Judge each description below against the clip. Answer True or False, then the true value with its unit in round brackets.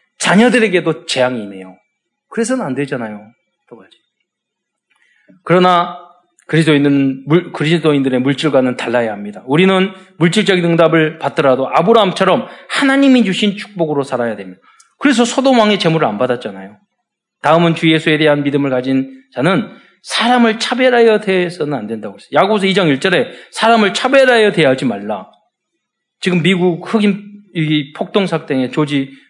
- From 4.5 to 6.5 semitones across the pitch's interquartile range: False (6.9 semitones)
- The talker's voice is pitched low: False (170 Hz)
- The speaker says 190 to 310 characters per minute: False (350 characters per minute)